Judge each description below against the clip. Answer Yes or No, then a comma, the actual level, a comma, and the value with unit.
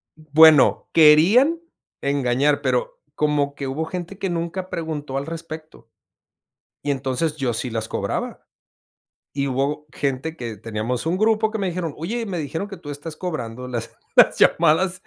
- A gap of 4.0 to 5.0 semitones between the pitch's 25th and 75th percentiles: Yes, average, 4.3 semitones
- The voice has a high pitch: No, medium, 155 Hz